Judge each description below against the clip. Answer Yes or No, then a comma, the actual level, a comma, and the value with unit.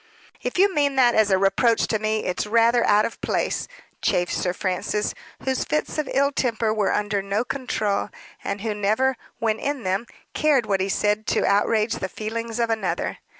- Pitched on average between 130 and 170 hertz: No, high, 220 Hz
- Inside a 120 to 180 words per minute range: No, average, 190 wpm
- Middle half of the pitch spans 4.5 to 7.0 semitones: No, average, 3.0 semitones